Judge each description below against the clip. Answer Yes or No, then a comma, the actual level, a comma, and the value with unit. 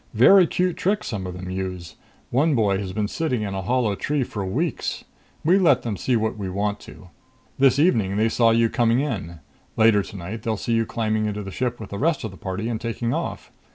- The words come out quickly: Yes, fast, 225 wpm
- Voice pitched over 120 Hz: No, low, 110 Hz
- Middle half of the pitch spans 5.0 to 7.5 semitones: No, average, 4.2 semitones